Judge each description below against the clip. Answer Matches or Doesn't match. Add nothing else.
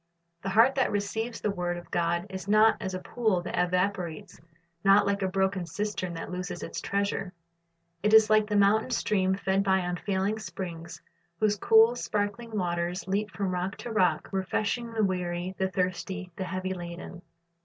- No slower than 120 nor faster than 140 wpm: Doesn't match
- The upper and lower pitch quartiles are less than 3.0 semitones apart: Matches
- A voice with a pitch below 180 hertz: Doesn't match